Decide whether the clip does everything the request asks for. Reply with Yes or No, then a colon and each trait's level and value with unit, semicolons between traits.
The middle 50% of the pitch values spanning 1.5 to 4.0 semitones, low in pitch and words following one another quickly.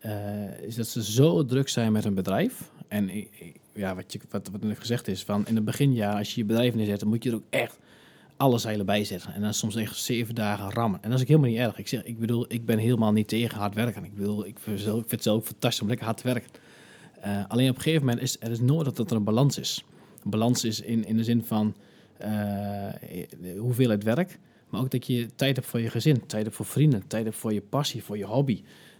Yes: average, 2.7 semitones; low, 115 Hz; fast, 265 wpm